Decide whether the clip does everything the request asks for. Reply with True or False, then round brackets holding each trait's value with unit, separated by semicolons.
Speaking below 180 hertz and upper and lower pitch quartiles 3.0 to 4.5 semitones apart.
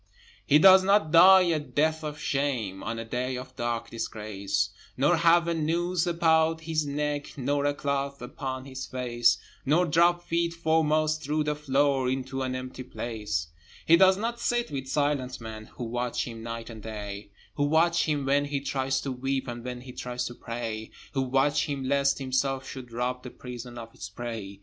True (135 Hz; 4.2 semitones)